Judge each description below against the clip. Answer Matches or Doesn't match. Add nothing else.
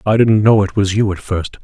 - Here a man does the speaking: Matches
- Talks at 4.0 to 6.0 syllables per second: Matches